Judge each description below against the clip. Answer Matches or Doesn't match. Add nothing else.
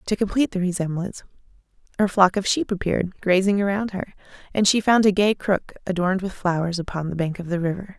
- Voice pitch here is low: Doesn't match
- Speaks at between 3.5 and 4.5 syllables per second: Doesn't match